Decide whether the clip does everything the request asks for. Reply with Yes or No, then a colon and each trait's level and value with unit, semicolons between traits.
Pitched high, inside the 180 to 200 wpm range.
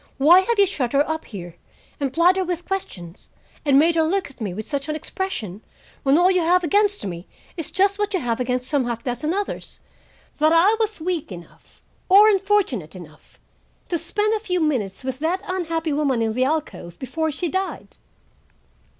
Yes: very high, 315 Hz; average, 190 wpm